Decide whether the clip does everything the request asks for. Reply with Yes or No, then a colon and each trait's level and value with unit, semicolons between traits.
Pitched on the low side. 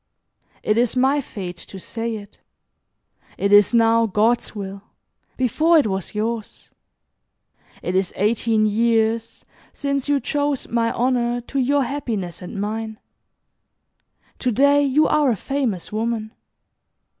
No: high, 230 Hz